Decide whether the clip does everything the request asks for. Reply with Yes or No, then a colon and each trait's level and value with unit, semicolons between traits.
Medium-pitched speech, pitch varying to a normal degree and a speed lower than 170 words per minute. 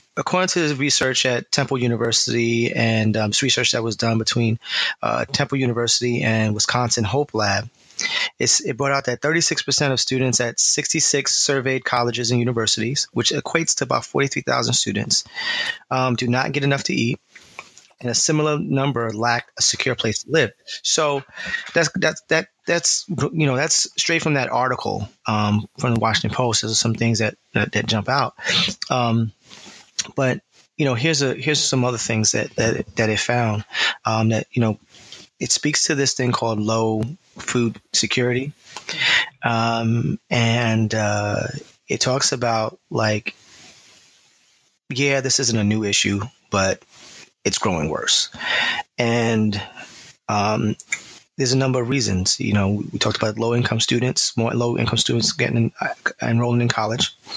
No: low, 120 Hz; average, 3.3 semitones; average, 160 wpm